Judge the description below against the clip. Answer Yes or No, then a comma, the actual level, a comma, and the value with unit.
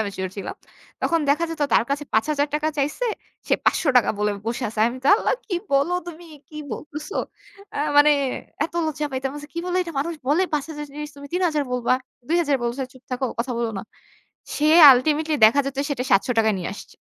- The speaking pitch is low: No, very high, 285 Hz